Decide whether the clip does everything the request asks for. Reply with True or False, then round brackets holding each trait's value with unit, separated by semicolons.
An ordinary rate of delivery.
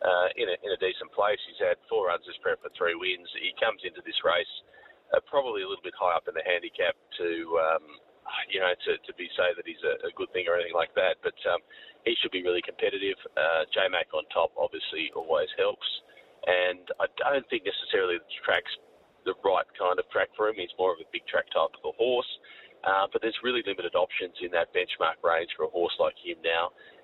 False (230 wpm)